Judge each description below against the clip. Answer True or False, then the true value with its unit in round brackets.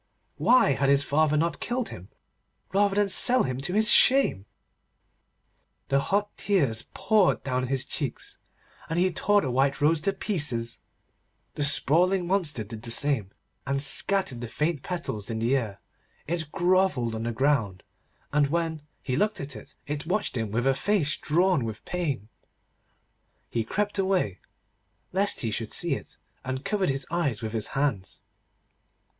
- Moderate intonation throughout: False (7.2 semitones)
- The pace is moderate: True (160 wpm)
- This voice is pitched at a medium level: True (145 Hz)